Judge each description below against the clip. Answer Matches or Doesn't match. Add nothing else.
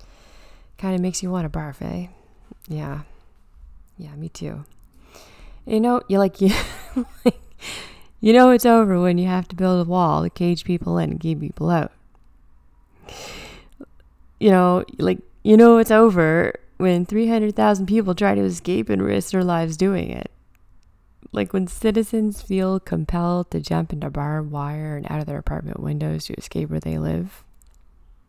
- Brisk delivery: Doesn't match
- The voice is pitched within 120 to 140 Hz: Doesn't match